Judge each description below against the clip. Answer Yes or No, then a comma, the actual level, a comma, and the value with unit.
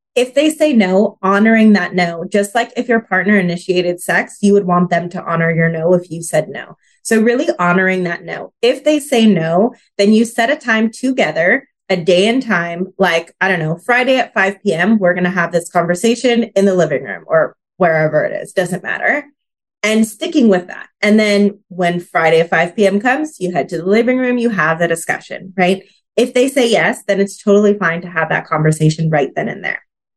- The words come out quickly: Yes, fast, 215 wpm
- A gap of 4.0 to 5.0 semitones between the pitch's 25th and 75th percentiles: Yes, average, 4.7 semitones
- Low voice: No, high, 195 Hz